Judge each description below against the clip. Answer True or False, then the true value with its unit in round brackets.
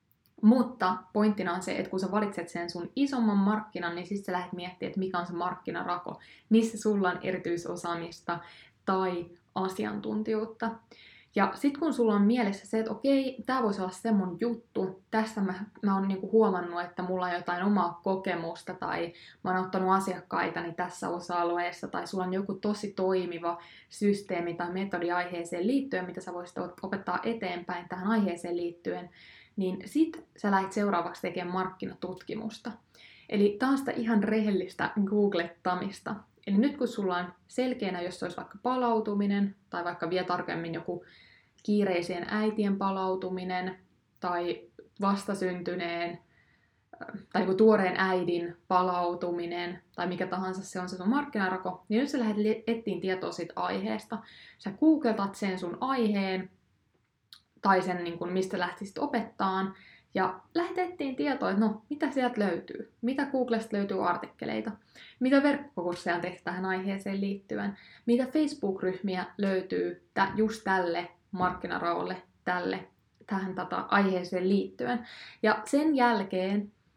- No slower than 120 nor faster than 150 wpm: True (140 wpm)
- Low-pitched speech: False (190 Hz)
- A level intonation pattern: False (3.3 semitones)